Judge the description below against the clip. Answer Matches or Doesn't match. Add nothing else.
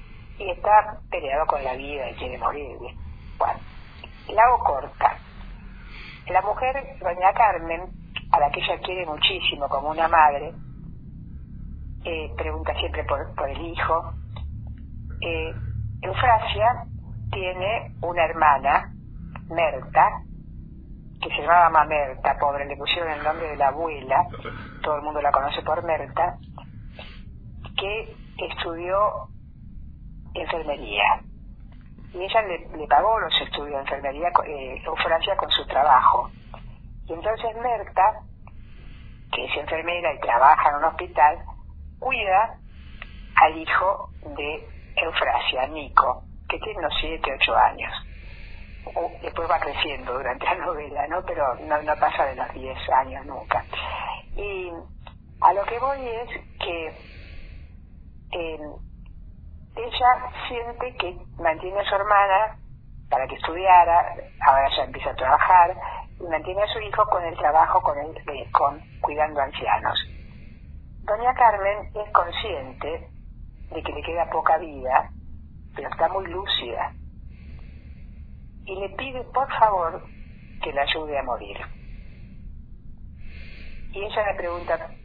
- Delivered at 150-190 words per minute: Doesn't match